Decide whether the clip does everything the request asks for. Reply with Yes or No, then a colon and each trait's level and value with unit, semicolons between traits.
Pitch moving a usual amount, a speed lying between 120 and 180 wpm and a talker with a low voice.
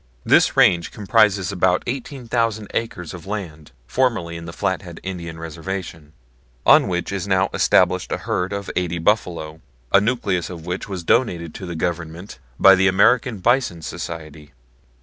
Yes: average, 3.3 semitones; average, 150 wpm; very low, 90 Hz